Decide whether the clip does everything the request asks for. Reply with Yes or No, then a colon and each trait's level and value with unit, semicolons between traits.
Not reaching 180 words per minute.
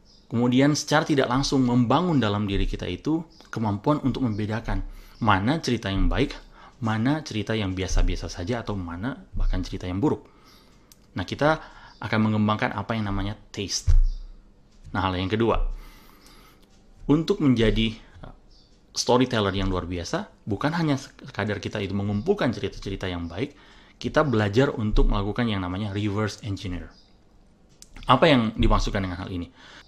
Yes: average, 135 wpm